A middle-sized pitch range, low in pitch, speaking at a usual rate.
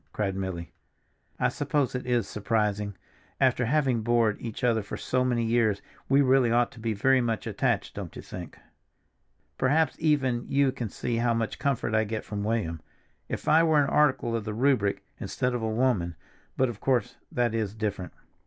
Yes: average, 3.4 semitones; low, 120 Hz; average, 180 wpm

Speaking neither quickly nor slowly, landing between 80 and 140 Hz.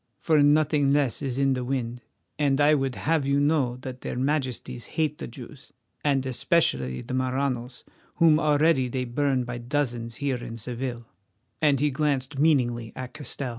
Yes: average, 170 wpm; low, 135 Hz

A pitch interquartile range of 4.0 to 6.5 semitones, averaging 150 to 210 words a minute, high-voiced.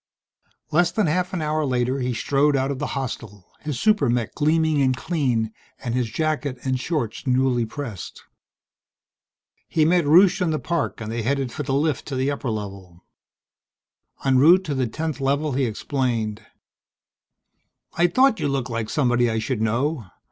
No: average, 4.4 semitones; average, 170 wpm; low, 135 Hz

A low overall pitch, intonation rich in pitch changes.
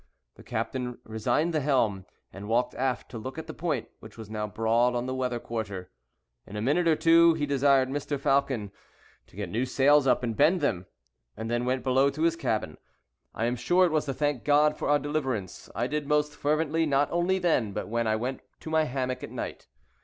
No: low, 130 Hz; average, 4.5 semitones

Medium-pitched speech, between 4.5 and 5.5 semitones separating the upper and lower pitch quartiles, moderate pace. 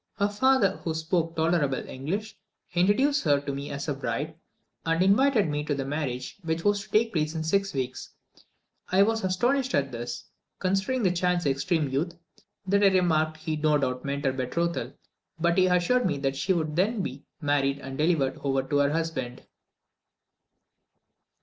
Yes: medium, 160 Hz; average, 5.2 semitones; average, 175 wpm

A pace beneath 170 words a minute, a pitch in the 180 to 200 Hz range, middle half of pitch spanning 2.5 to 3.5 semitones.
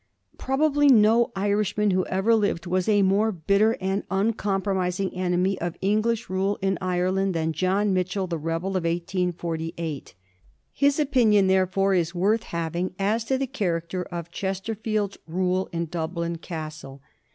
Yes: average, 145 wpm; high, 190 Hz; average, 3.2 semitones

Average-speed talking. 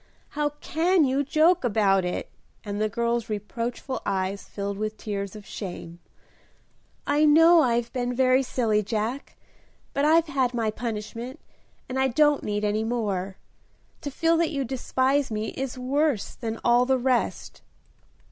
Yes: average, 150 wpm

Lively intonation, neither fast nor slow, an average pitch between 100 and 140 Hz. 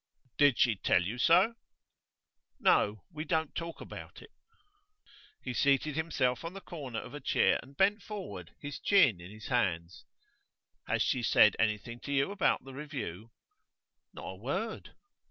Yes: wide, 6.5 semitones; average, 155 wpm; low, 135 Hz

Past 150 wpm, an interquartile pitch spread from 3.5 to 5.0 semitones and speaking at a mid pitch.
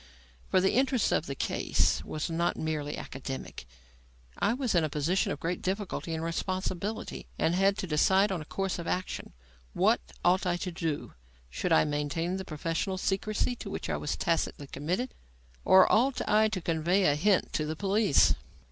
Yes: average, 180 wpm; average, 4.0 semitones; medium, 175 Hz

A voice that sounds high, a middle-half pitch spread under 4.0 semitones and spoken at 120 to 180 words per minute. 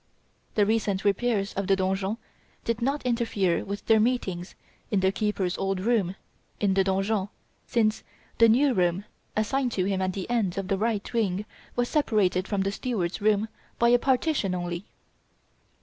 Yes: high, 205 Hz; average, 3.3 semitones; average, 165 wpm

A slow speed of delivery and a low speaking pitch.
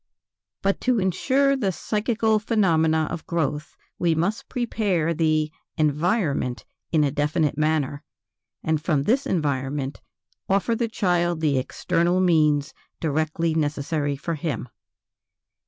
No: slow, 120 wpm; medium, 160 Hz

